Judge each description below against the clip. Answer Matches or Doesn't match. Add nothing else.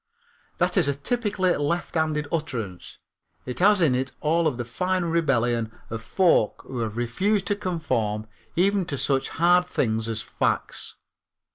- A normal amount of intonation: Doesn't match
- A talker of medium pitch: Matches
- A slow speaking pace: Doesn't match